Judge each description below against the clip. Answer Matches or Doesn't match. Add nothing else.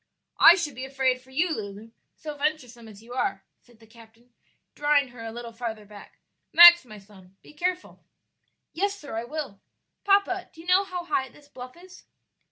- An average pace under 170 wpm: Doesn't match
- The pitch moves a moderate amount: Doesn't match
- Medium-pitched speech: Doesn't match